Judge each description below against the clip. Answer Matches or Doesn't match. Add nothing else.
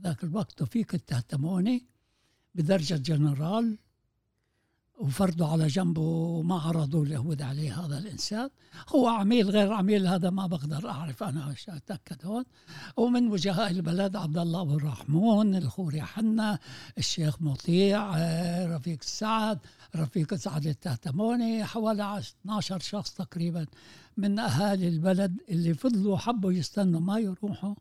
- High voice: Doesn't match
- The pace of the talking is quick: Doesn't match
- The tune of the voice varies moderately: Matches